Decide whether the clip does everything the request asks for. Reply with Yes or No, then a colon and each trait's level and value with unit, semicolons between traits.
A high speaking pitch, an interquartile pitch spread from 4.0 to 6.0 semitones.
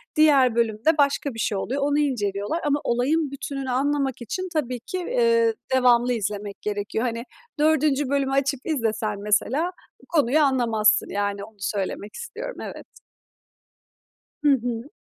Yes: very high, 260 Hz; average, 5.0 semitones